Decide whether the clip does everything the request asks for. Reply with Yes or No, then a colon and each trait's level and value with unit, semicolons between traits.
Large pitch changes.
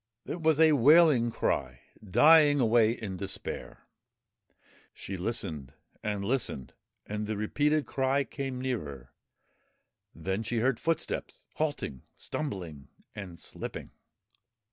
Yes: wide, 6.9 semitones